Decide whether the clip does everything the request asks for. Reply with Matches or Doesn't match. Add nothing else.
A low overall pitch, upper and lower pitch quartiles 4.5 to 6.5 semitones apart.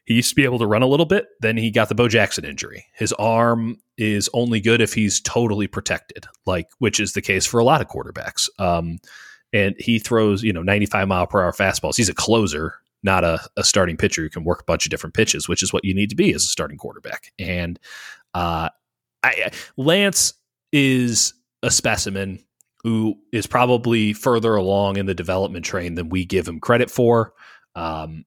Doesn't match